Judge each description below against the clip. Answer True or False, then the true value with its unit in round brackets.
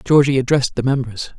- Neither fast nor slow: True (175 wpm)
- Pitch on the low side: True (130 Hz)